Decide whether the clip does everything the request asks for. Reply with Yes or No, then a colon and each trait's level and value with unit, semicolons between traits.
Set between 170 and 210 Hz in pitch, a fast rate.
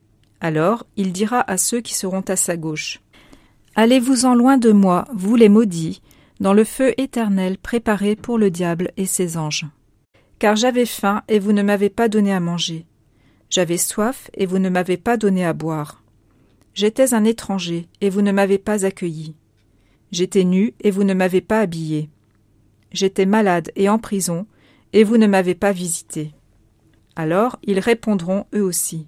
No: high, 190 Hz; average, 170 wpm